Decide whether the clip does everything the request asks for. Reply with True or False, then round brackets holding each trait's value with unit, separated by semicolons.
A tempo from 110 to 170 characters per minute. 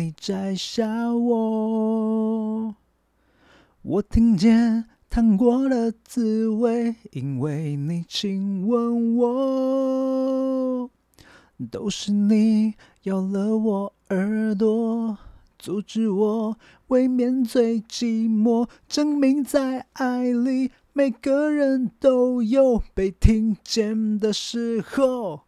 True (115 characters per minute)